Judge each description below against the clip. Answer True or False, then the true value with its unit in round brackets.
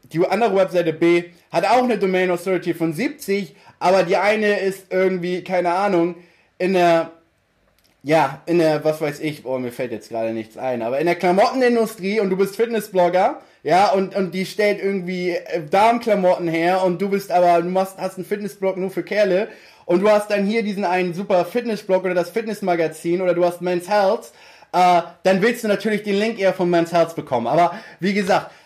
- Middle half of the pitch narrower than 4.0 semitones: True (2.8 semitones)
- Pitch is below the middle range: False (185 Hz)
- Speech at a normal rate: False (195 wpm)